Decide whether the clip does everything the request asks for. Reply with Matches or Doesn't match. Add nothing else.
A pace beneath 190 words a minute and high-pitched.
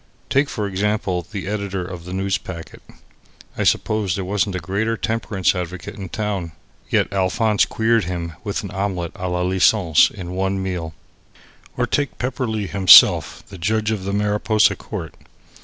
Doesn't match